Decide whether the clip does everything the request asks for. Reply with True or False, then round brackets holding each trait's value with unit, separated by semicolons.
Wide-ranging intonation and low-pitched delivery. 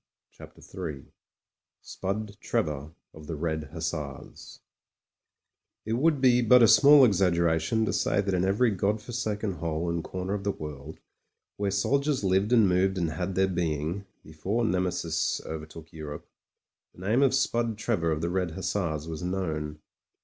False (4.9 semitones; 95 Hz)